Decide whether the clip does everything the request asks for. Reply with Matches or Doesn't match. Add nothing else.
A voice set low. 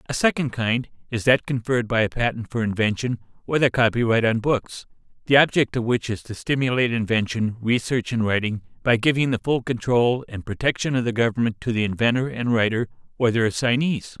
Matches